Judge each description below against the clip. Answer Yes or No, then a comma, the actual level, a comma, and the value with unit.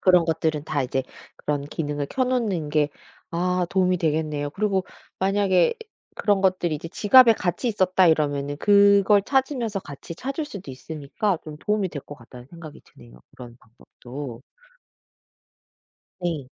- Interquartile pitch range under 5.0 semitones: No, wide, 5.4 semitones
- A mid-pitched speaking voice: Yes, medium, 170 Hz